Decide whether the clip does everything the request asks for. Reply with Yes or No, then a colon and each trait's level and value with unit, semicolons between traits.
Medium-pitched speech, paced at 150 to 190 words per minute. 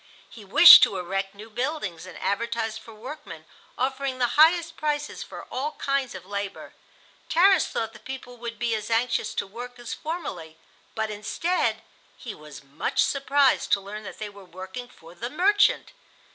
No: high, 230 Hz; average, 170 wpm